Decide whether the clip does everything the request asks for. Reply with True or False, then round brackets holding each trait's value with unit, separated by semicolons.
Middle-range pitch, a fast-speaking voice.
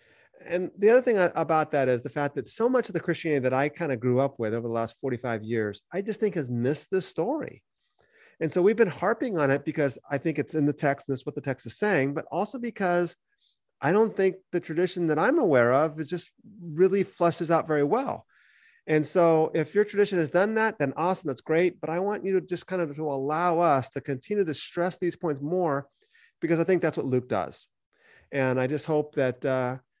True (160 Hz; 235 wpm)